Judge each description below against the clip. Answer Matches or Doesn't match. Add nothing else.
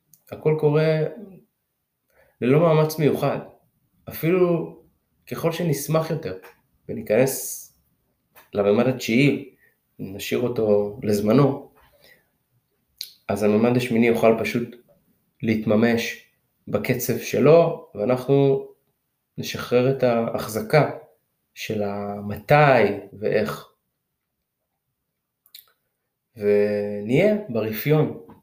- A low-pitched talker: Matches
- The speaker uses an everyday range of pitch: Doesn't match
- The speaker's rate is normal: Doesn't match